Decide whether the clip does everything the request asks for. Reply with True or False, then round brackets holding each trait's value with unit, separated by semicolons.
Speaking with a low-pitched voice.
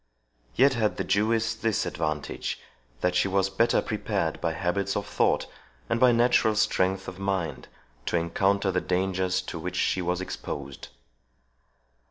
True (95 Hz)